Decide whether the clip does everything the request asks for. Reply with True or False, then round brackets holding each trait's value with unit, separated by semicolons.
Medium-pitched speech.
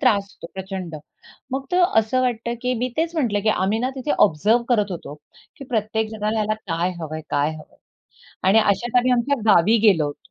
False (215 Hz)